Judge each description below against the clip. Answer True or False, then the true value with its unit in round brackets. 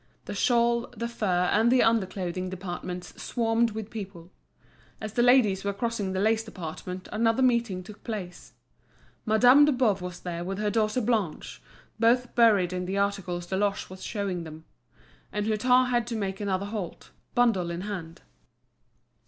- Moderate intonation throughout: True (3.9 semitones)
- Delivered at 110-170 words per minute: True (160 wpm)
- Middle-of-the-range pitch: False (205 Hz)